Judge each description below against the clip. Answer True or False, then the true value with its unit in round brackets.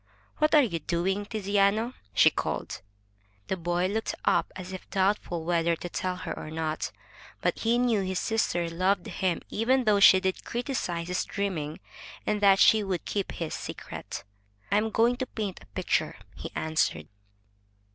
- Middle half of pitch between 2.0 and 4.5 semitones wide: True (3.8 semitones)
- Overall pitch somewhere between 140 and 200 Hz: True (190 Hz)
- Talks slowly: False (165 wpm)